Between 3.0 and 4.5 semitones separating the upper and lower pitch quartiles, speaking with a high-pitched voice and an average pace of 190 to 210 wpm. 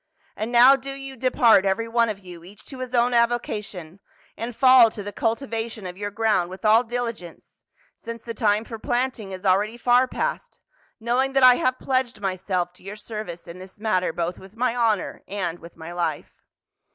Yes: average, 4.2 semitones; high, 220 Hz; average, 200 wpm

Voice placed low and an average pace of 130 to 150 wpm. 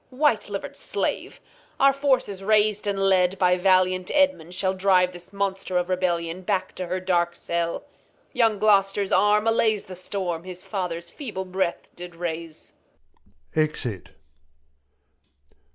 No: medium, 185 Hz; average, 140 wpm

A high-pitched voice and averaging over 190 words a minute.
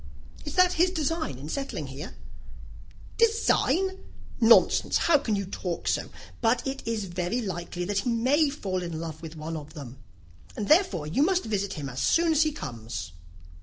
No: high, 205 Hz; average, 175 wpm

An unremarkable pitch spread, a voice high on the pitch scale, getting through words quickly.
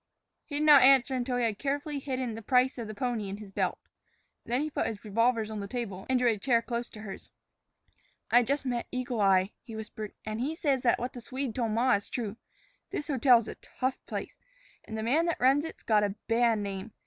Yes: average, 3.3 semitones; high, 240 Hz; fast, 230 wpm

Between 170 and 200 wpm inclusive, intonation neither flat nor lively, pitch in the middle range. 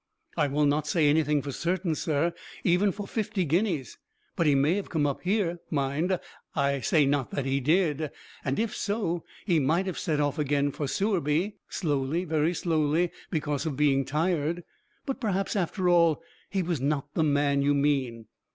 Yes: average, 180 wpm; average, 3.8 semitones; medium, 155 Hz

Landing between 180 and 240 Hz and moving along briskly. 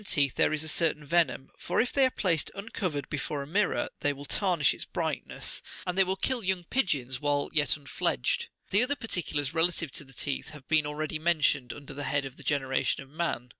No: medium, 150 Hz; fast, 220 wpm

